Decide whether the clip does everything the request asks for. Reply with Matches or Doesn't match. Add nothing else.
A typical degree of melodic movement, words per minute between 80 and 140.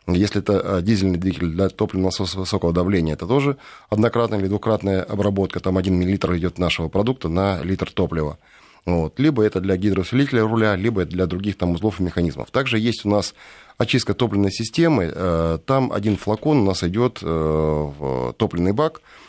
Doesn't match